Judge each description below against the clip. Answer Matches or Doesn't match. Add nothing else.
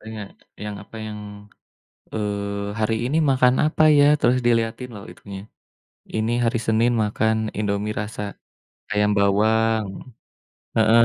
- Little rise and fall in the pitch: Matches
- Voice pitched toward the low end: Matches